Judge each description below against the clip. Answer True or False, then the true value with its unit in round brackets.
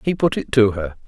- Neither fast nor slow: False (280 wpm)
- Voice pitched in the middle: False (115 Hz)